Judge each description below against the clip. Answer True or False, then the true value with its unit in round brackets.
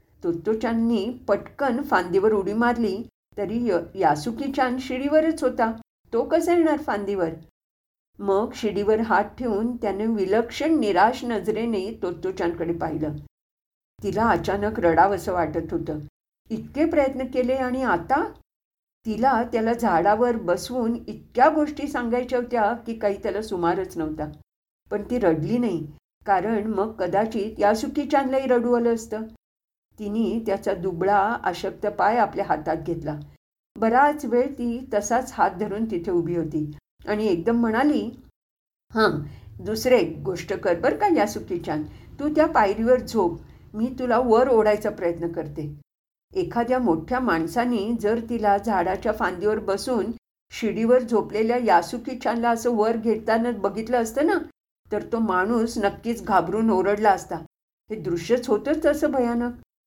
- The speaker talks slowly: True (130 wpm)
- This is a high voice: True (220 Hz)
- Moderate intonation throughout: True (3.8 semitones)